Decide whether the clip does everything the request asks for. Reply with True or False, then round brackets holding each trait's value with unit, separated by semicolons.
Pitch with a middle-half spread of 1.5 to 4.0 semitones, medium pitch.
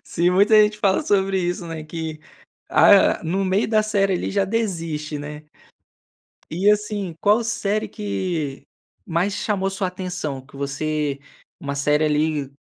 False (4.7 semitones; 180 Hz)